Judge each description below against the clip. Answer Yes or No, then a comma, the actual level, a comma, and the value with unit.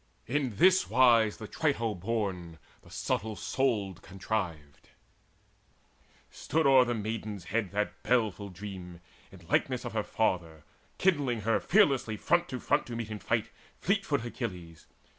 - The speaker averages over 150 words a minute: No, average, 140 wpm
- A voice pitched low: Yes, low, 110 Hz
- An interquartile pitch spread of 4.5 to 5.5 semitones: Yes, average, 5.0 semitones